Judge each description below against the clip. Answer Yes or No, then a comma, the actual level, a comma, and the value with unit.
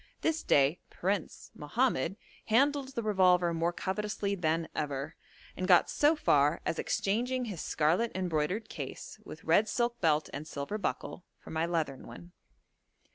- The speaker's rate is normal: Yes, average, 145 wpm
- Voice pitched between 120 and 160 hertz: No, medium, 185 Hz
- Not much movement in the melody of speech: No, wide, 5.6 semitones